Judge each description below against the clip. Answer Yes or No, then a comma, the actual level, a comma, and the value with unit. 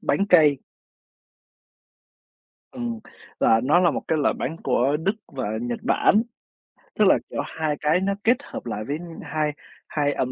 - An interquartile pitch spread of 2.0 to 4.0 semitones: No, average, 4.9 semitones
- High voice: No, medium, 150 Hz